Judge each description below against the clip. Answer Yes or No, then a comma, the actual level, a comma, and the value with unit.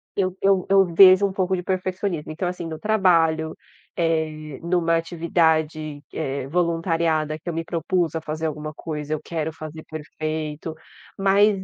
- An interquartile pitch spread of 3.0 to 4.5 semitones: No, narrow, 2.6 semitones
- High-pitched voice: No, medium, 165 Hz